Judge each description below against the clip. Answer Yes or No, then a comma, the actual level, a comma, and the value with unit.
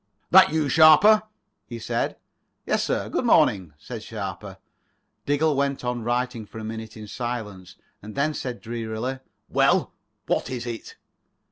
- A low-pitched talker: Yes, low, 120 Hz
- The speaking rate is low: No, average, 145 wpm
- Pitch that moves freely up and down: No, average, 3.8 semitones